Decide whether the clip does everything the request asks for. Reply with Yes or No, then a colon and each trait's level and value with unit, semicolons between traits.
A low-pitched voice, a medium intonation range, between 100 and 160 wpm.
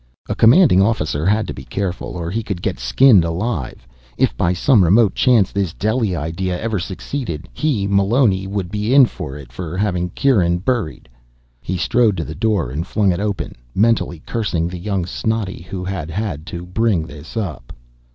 No: very low, 95 Hz; average, 4.4 semitones; average, 180 wpm